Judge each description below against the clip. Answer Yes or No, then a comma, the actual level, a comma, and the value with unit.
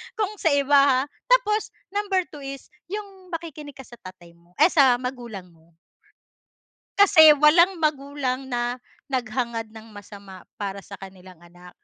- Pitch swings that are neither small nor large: No, wide, 7.8 semitones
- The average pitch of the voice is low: No, very high, 260 Hz